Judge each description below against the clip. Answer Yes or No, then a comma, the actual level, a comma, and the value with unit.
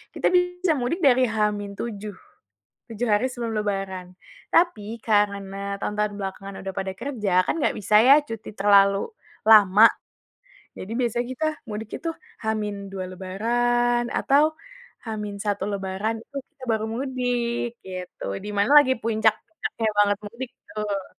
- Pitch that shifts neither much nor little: Yes, average, 3.3 semitones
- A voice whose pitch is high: Yes, high, 215 Hz